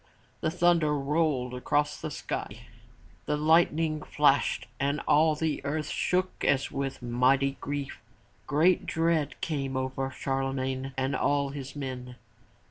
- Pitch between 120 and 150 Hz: Yes, medium, 140 Hz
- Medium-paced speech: No, slow, 130 wpm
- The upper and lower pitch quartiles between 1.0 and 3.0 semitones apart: Yes, narrow, 2.5 semitones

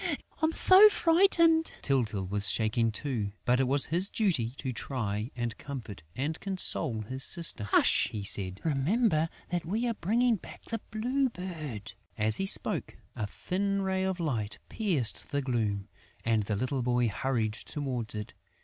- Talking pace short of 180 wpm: Yes, average, 160 wpm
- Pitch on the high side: No, low, 135 Hz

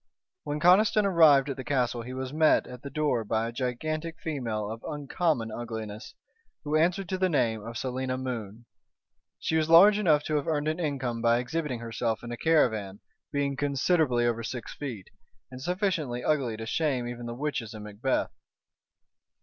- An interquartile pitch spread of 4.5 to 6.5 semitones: Yes, average, 4.9 semitones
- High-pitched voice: No, low, 130 Hz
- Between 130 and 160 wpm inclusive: No, average, 175 wpm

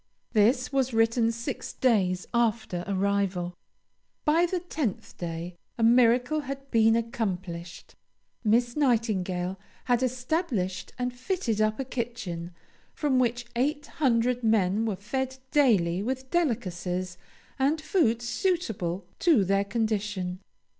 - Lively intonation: No, average, 5.0 semitones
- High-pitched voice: Yes, high, 230 Hz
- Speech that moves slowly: Yes, slow, 120 wpm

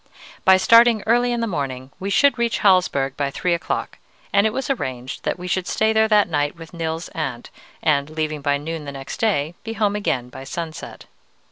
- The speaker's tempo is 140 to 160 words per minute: No, fast, 205 wpm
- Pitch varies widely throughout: Yes, wide, 7.1 semitones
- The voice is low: No, medium, 170 Hz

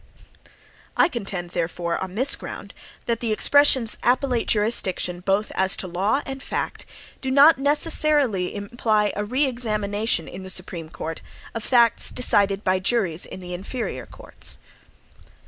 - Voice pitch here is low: No, high, 210 Hz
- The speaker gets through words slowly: No, average, 145 wpm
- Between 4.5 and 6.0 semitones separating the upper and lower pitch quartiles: Yes, average, 4.9 semitones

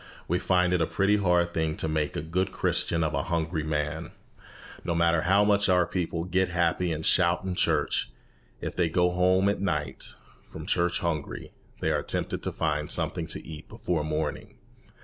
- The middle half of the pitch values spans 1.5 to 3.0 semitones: Yes, narrow, 2.4 semitones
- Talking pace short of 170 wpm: No, average, 190 wpm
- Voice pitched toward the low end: Yes, very low, 85 Hz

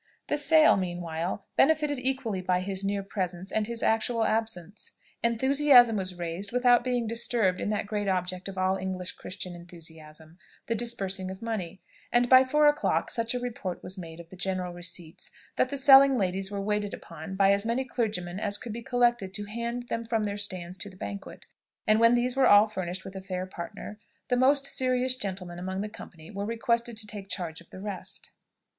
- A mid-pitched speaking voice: No, high, 205 Hz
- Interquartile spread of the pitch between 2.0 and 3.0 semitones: No, average, 4.4 semitones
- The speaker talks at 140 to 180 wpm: No, average, 195 wpm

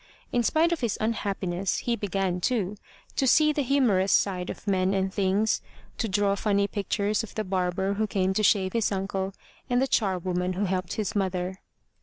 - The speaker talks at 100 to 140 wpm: No, average, 185 wpm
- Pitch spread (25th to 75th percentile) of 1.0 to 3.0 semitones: Yes, narrow, 2.5 semitones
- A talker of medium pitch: No, high, 200 Hz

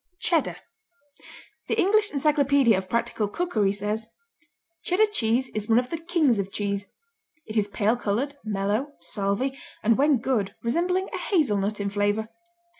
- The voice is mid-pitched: No, high, 230 Hz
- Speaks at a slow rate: No, average, 145 wpm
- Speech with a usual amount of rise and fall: No, wide, 5.9 semitones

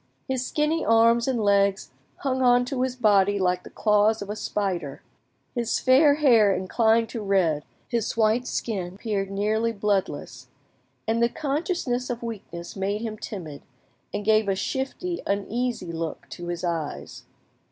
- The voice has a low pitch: No, high, 215 Hz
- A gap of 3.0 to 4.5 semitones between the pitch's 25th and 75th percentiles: Yes, average, 3.9 semitones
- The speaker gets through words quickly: No, average, 150 wpm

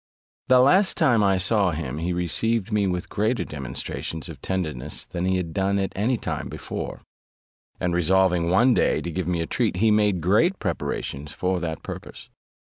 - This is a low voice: Yes, very low, 95 Hz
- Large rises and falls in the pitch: No, average, 4.0 semitones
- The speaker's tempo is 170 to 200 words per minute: Yes, average, 180 wpm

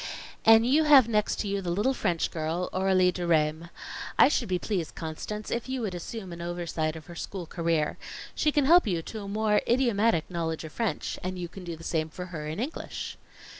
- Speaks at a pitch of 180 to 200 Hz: Yes, medium, 185 Hz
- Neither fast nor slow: No, fast, 210 wpm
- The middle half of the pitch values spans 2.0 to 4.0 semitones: No, average, 4.9 semitones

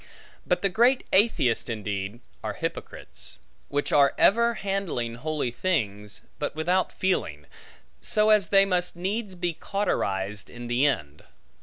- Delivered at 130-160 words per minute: Yes, slow, 135 wpm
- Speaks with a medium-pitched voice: Yes, medium, 160 Hz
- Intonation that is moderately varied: No, wide, 9.0 semitones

